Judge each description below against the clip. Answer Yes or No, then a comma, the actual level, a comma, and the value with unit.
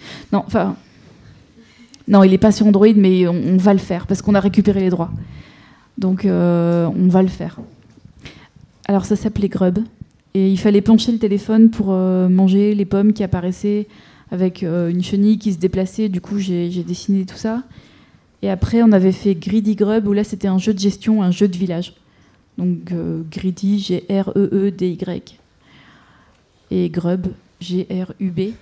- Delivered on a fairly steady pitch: Yes, narrow, 2.3 semitones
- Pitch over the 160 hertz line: Yes, high, 190 Hz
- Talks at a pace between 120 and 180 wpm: Yes, average, 170 wpm